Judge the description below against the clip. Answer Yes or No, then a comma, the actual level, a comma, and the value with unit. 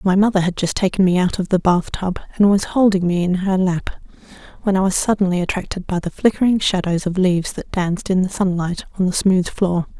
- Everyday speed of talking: No, fast, 230 wpm